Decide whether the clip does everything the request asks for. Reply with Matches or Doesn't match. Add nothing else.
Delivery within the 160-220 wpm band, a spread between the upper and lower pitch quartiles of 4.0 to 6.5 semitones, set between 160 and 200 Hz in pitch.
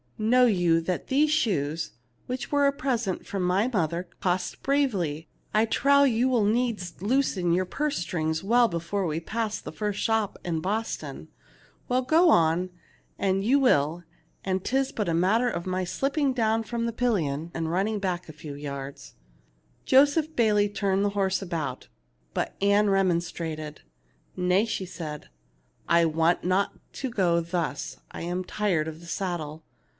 Matches